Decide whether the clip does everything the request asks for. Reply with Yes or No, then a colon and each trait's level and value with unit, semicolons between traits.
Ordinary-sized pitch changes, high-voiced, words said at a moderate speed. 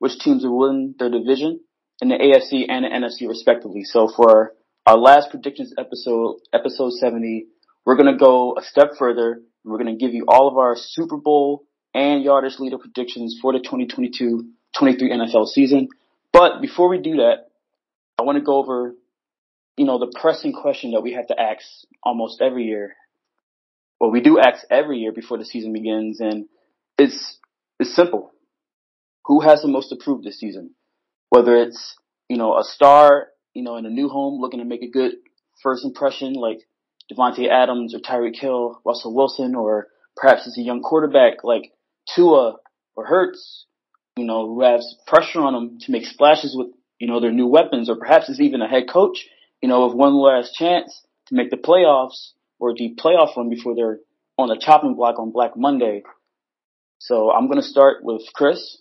No: average, 3.7 semitones; low, 130 Hz; average, 190 wpm